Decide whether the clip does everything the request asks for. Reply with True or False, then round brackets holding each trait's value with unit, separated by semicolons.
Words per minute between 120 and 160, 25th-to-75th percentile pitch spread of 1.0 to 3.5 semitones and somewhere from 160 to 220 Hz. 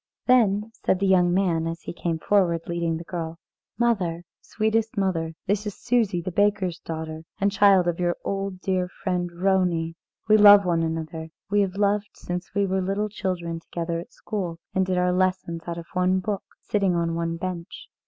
False (190 wpm; 2.9 semitones; 185 Hz)